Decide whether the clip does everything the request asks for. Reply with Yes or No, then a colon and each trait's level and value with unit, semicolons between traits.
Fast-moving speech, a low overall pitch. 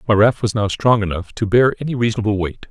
Yes: fast, 245 wpm; low, 110 Hz